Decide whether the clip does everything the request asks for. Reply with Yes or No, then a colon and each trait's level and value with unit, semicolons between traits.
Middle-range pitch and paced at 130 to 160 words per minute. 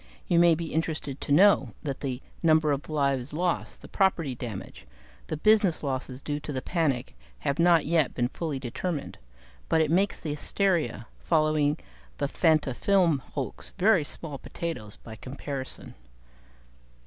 Yes: medium, 150 Hz; average, 150 wpm